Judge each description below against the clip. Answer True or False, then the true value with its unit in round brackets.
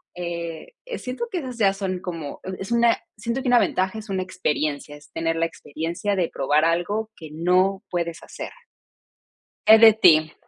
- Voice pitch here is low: False (185 Hz)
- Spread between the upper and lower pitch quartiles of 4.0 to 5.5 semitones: True (4.9 semitones)